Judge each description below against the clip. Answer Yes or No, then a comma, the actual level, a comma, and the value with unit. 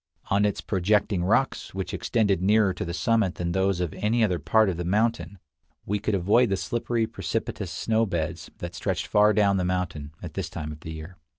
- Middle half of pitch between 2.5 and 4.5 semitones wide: Yes, average, 3.6 semitones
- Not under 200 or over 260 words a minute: Yes, fast, 205 wpm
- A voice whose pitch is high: No, very low, 95 Hz